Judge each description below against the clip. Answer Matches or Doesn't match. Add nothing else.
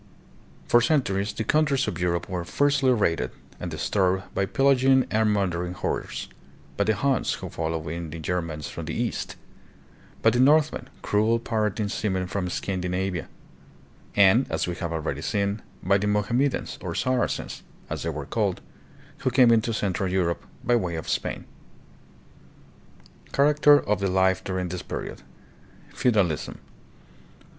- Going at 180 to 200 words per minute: Doesn't match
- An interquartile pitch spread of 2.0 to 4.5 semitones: Doesn't match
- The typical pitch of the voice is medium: Doesn't match